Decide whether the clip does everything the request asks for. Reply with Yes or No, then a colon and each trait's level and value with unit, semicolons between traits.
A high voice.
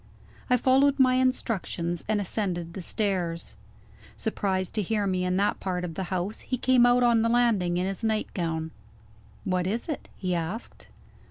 Yes: high, 195 Hz